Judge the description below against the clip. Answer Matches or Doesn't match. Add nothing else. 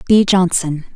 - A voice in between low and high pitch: Matches